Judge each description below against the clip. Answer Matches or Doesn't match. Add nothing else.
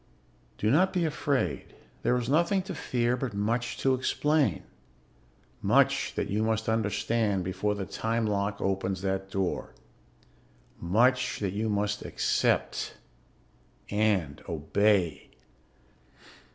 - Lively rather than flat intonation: Doesn't match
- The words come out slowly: Matches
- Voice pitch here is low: Matches